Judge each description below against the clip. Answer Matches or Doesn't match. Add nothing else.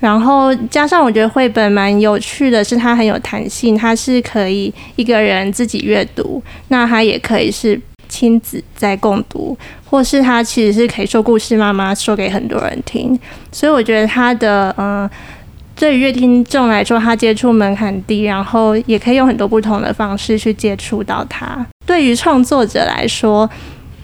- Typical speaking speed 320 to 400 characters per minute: Doesn't match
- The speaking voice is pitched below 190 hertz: Doesn't match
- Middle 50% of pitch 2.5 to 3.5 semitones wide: Matches